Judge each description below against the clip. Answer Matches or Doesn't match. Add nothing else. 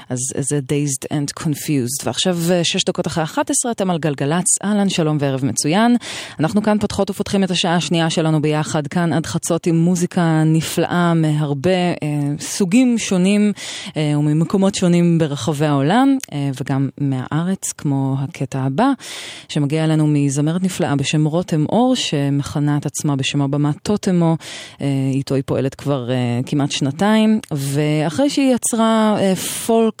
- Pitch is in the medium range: Matches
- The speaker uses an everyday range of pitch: Matches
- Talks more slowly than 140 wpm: Doesn't match